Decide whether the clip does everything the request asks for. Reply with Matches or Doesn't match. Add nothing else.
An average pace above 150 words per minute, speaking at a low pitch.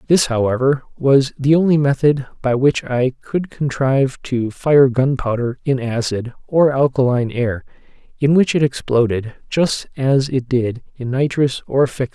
Matches